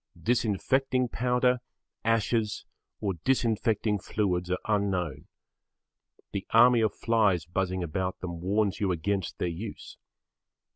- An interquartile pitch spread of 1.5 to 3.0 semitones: No, average, 3.9 semitones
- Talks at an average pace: No, slow, 110 wpm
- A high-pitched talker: No, low, 105 Hz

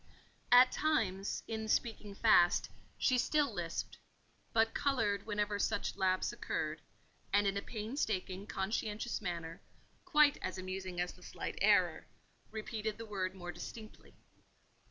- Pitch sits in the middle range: No, high, 210 Hz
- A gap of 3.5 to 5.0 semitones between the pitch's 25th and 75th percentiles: No, average, 3.1 semitones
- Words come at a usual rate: No, slow, 130 wpm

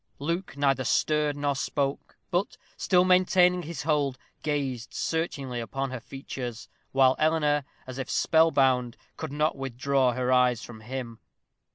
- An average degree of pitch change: Yes, average, 3.2 semitones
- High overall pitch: No, low, 135 Hz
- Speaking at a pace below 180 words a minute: Yes, average, 145 wpm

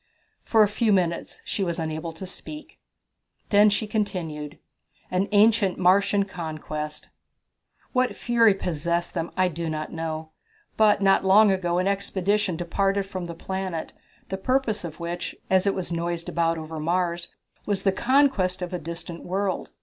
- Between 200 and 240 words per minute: No, average, 155 wpm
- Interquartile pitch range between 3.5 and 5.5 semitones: No, average, 3.1 semitones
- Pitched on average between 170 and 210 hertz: Yes, medium, 185 Hz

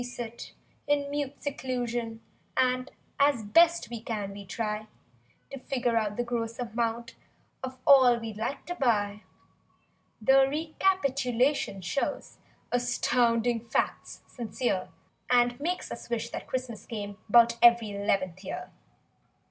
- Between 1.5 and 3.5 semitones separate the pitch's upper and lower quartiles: Yes, average, 2.8 semitones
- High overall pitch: Yes, high, 240 Hz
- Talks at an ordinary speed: No, slow, 130 wpm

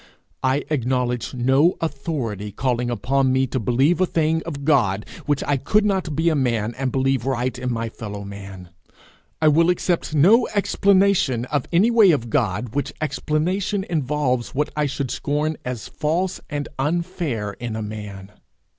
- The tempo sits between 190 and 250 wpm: No, average, 165 wpm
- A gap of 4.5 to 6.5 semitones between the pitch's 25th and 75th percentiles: Yes, average, 5.0 semitones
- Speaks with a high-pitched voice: No, low, 135 Hz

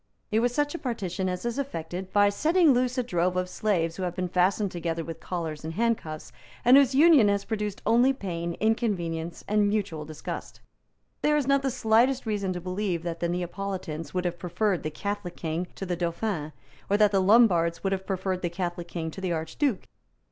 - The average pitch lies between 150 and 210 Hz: Yes, high, 190 Hz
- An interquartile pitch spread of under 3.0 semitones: No, average, 4.4 semitones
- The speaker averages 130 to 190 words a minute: No, average, 200 wpm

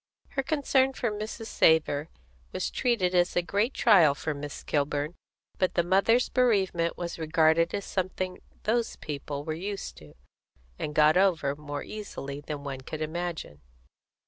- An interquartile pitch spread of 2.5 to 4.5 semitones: No, average, 5.3 semitones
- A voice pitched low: No, medium, 170 Hz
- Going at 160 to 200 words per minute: No, average, 150 wpm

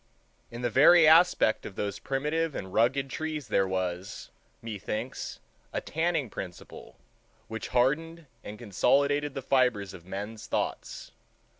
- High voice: No, low, 125 Hz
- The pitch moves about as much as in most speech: No, wide, 6.3 semitones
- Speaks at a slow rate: Yes, slow, 130 wpm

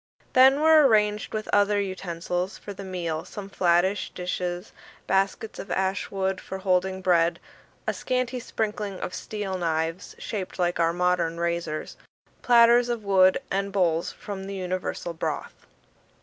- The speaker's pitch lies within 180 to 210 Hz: Yes, high, 190 Hz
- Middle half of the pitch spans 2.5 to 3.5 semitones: Yes, average, 2.8 semitones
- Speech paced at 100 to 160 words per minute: Yes, average, 145 wpm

